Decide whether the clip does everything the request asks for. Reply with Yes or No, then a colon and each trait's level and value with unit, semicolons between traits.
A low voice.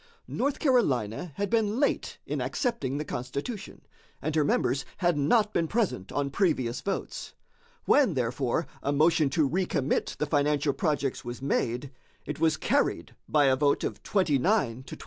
No: medium, 150 Hz